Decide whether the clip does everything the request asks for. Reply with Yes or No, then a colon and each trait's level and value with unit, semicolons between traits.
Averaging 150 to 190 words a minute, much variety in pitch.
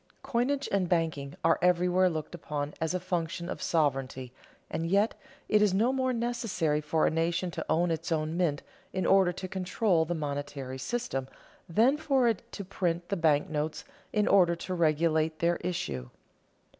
No: average, 170 wpm; average, 3.6 semitones